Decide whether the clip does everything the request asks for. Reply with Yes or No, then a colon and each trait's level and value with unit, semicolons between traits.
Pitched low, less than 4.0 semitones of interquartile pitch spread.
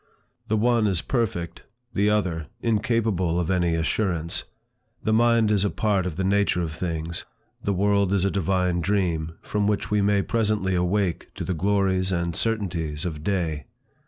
Yes: very low, 95 Hz; average, 3.4 semitones